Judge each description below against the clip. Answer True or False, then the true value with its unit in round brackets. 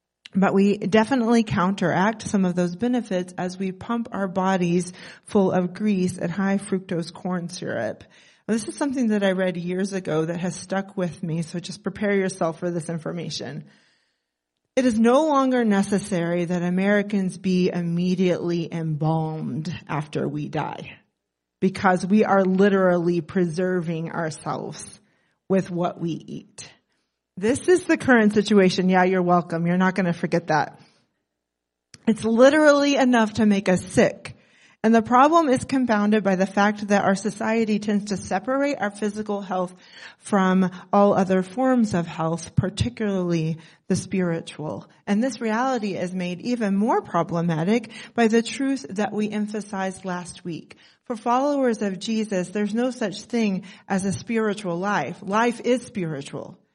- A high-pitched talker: True (195 Hz)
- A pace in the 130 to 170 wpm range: True (150 wpm)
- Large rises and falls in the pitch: False (3.6 semitones)